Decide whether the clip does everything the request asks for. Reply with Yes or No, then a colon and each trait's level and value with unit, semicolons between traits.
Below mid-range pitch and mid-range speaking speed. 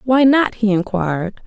No: high, 215 Hz; average, 165 wpm